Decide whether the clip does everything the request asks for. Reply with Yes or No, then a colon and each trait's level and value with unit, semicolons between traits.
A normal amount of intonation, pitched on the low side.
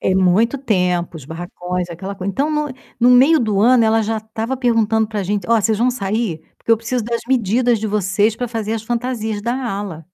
No: average, 3.5 semitones; high, 220 Hz